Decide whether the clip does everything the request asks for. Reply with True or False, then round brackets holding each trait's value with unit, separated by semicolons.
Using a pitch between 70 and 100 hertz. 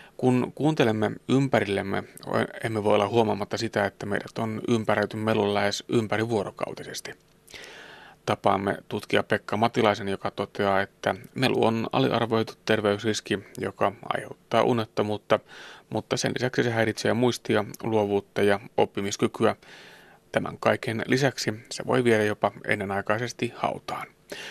False (110 Hz)